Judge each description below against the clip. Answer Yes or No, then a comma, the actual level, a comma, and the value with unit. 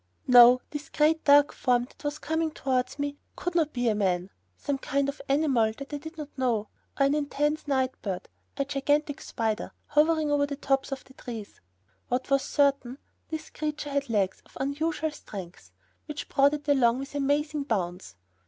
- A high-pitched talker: Yes, very high, 280 Hz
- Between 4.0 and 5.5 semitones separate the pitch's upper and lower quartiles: No, average, 3.2 semitones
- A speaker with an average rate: Yes, average, 180 wpm